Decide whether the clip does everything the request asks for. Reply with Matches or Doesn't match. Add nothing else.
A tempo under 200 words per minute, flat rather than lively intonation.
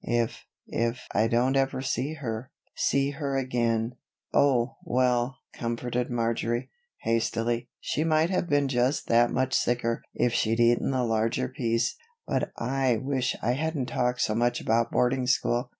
Matches